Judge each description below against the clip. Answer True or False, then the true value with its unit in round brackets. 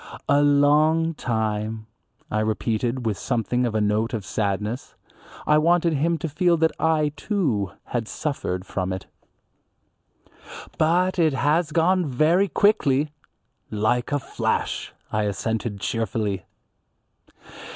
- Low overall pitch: True (130 Hz)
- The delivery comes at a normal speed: False (120 wpm)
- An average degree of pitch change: False (6.7 semitones)